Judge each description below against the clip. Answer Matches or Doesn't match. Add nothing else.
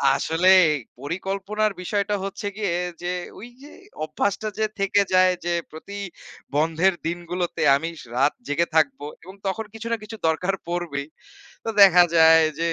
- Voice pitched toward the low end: Doesn't match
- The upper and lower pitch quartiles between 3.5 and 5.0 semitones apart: Matches